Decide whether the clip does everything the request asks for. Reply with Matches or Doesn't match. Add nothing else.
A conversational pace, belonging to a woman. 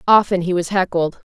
Matches